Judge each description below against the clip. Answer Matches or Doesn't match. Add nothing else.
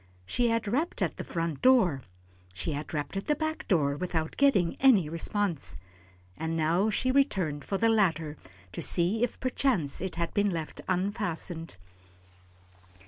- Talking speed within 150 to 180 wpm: Matches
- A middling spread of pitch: Doesn't match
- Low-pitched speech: Doesn't match